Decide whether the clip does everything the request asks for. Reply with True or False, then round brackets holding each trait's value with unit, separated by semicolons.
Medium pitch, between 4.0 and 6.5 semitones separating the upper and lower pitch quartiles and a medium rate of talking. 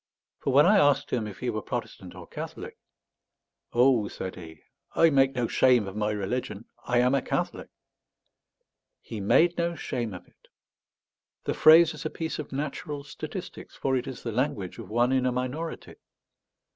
False (125 Hz; 4.7 semitones; 175 wpm)